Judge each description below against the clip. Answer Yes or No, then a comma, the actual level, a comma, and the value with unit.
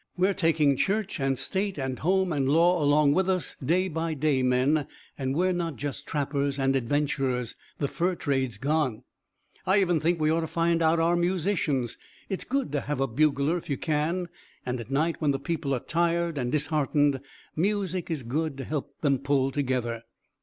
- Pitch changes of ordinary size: Yes, average, 3.9 semitones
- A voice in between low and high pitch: Yes, medium, 150 Hz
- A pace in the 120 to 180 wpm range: No, average, 190 wpm